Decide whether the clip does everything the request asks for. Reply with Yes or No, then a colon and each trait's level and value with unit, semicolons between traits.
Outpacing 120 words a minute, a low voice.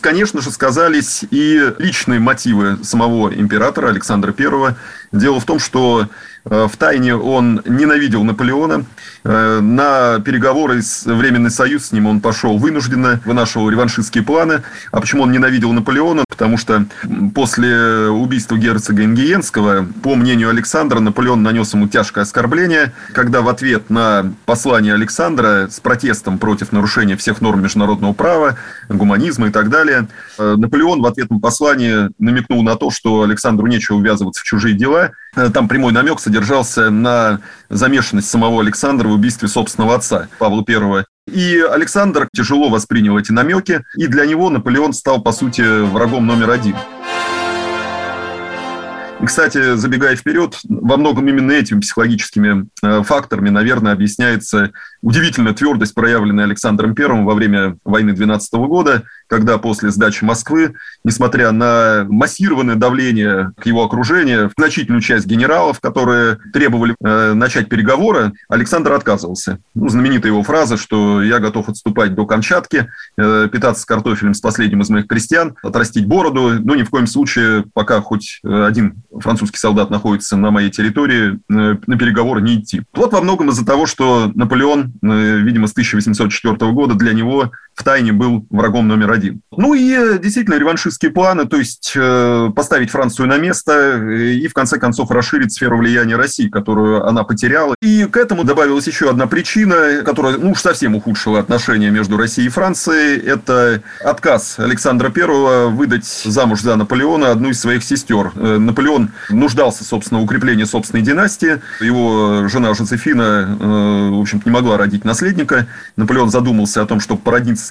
Yes: average, 150 wpm; low, 115 Hz